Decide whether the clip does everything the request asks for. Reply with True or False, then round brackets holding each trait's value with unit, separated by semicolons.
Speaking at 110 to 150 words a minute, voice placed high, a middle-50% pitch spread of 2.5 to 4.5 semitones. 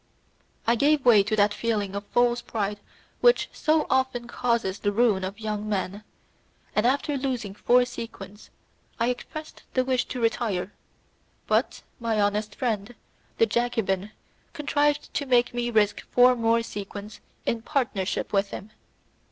True (145 wpm; 230 Hz; 3.2 semitones)